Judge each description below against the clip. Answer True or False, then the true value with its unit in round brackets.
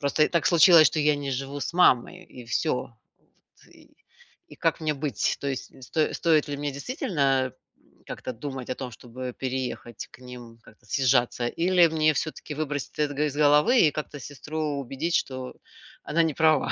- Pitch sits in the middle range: True (145 Hz)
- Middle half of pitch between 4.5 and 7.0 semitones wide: False (3.2 semitones)